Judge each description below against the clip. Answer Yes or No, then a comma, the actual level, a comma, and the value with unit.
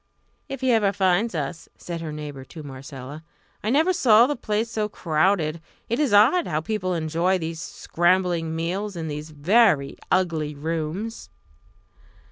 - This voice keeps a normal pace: Yes, average, 150 wpm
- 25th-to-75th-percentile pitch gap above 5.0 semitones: Yes, wide, 5.4 semitones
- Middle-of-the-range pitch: Yes, medium, 175 Hz